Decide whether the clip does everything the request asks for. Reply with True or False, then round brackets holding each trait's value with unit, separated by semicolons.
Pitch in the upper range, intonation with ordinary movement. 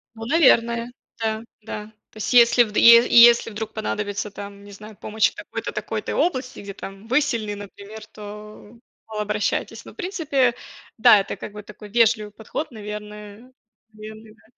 False (215 Hz; 2.0 semitones)